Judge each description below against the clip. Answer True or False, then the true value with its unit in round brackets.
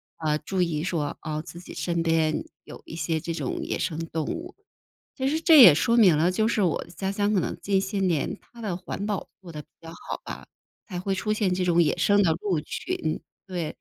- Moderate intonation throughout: True (3.9 semitones)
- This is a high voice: False (180 Hz)